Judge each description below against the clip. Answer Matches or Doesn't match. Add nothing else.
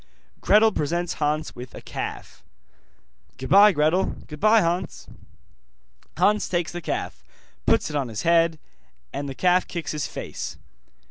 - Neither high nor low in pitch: Matches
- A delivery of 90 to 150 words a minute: Matches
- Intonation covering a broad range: Doesn't match